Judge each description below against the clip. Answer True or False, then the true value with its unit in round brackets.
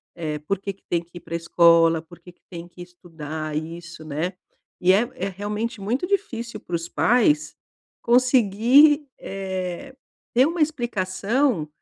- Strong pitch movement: True (6.0 semitones)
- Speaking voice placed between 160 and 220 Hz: True (190 Hz)